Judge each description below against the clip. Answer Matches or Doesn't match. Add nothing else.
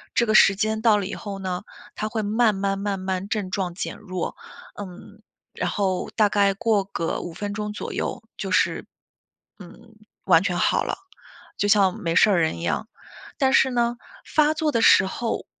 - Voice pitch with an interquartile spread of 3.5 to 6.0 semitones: Doesn't match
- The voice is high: Matches